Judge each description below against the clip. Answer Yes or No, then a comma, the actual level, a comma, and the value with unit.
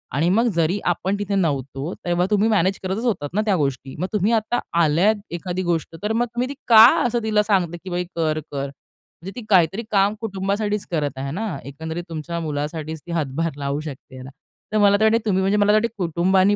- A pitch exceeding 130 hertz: Yes, medium, 185 Hz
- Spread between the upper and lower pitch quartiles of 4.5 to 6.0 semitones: Yes, average, 4.9 semitones